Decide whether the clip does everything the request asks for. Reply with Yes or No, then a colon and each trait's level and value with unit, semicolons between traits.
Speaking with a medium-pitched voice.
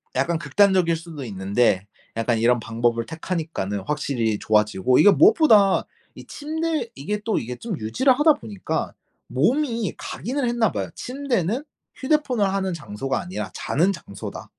Yes: medium, 170 Hz